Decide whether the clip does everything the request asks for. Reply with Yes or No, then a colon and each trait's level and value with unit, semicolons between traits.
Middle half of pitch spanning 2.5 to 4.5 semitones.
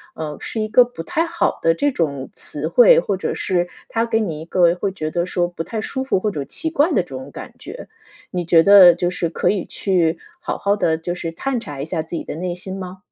Yes: average, 4.1 semitones